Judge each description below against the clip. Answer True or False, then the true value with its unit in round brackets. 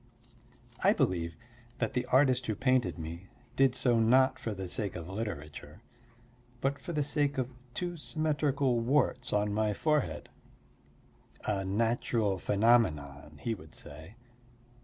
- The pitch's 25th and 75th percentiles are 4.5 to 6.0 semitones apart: True (5.5 semitones)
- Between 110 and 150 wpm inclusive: True (135 wpm)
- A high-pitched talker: False (115 Hz)